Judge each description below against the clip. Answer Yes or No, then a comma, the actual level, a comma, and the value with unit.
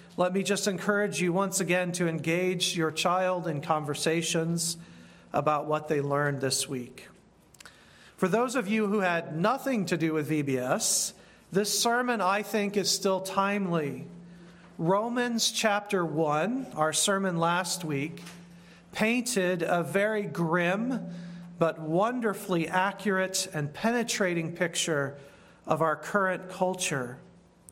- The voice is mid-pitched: Yes, medium, 180 Hz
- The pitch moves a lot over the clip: No, average, 3.5 semitones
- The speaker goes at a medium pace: No, slow, 125 wpm